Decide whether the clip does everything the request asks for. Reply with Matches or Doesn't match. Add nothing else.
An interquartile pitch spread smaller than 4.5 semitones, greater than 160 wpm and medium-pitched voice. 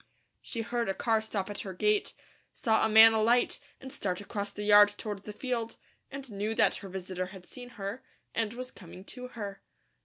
Doesn't match